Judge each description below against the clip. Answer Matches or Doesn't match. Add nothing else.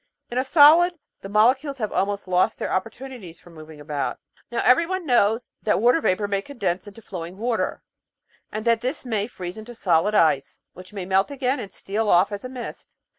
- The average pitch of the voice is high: Matches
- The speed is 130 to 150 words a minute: Doesn't match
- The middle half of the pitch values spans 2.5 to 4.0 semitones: Doesn't match